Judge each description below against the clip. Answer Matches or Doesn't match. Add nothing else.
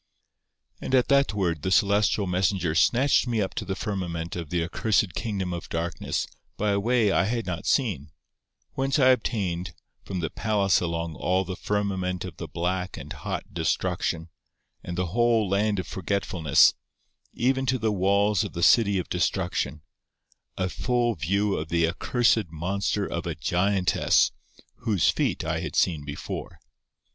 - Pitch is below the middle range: Matches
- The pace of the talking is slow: Doesn't match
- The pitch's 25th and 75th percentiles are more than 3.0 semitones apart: Matches